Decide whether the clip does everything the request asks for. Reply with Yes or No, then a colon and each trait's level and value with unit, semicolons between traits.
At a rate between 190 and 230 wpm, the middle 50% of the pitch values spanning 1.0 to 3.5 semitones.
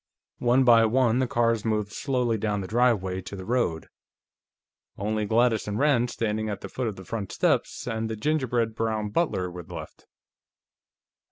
No: average, 170 wpm; average, 2.8 semitones